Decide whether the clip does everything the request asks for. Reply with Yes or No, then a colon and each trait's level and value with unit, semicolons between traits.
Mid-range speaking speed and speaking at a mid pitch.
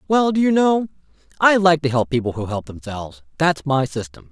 Yes: average, 195 wpm; medium, 145 Hz